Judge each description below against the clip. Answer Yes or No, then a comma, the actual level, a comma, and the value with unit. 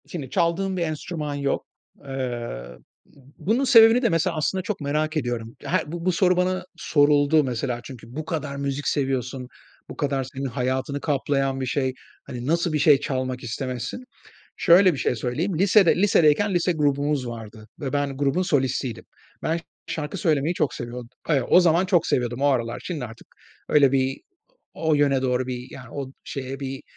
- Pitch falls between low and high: Yes, medium, 145 Hz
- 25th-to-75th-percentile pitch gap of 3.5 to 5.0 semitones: Yes, average, 4.2 semitones